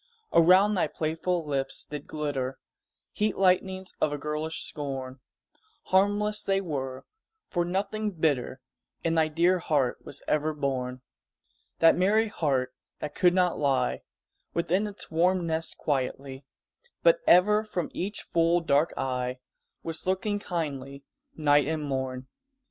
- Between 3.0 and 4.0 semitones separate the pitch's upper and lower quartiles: No, average, 5.0 semitones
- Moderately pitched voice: Yes, medium, 160 Hz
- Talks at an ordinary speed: No, slow, 130 wpm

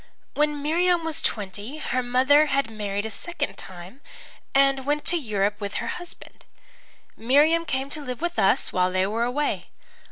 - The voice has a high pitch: Yes, very high, 265 Hz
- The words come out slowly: No, average, 165 wpm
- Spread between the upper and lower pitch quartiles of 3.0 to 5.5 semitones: No, wide, 6.1 semitones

